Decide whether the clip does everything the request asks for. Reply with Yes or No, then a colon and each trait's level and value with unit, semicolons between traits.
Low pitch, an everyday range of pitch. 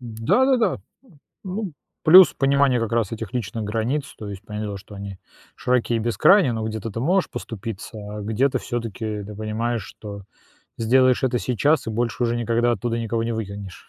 Yes: low, 115 Hz; average, 3.0 semitones